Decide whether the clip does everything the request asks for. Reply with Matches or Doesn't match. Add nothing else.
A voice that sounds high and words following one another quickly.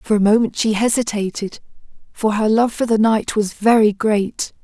Doesn't match